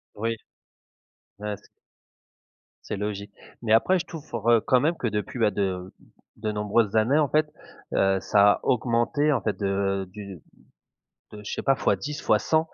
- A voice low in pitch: Yes, low, 110 Hz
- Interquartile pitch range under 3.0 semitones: No, average, 4.1 semitones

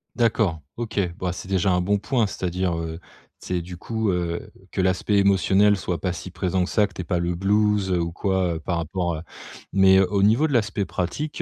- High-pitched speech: No, very low, 95 Hz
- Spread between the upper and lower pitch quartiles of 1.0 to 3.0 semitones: Yes, narrow, 2.6 semitones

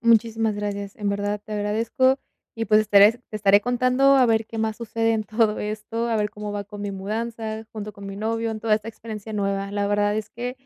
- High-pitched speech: Yes, high, 215 Hz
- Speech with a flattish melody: Yes, narrow, 1.7 semitones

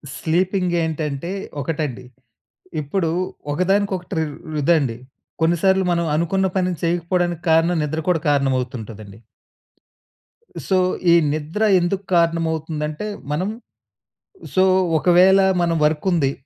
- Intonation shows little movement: No, average, 3.3 semitones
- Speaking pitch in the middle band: Yes, medium, 165 Hz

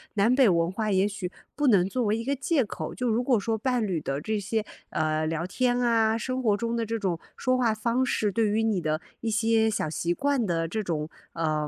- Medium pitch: No, high, 220 Hz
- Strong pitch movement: No, average, 4.6 semitones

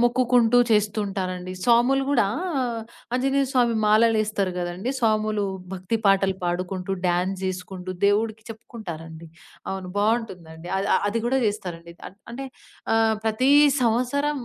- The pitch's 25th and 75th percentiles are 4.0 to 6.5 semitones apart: Yes, average, 4.3 semitones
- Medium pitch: No, high, 210 Hz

